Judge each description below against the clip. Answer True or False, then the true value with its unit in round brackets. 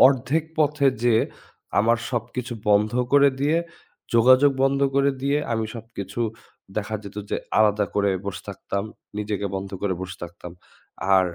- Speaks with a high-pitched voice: False (110 Hz)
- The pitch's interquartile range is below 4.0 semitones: False (5.2 semitones)